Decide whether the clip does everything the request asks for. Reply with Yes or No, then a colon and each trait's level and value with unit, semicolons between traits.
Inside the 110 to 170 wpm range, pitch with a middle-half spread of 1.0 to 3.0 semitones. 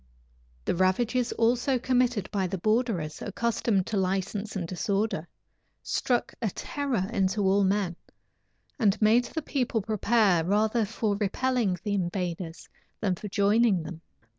No: slow, 135 wpm; average, 3.7 semitones